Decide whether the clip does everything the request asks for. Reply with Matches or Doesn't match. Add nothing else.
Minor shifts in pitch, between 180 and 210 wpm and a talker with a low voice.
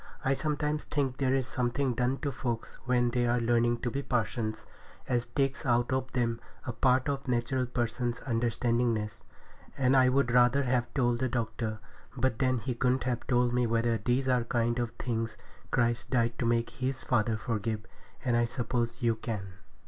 Matches